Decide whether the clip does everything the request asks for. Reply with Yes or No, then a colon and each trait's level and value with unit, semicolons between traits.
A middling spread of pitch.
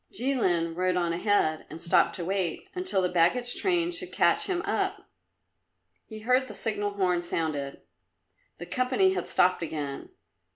No: wide, 6.9 semitones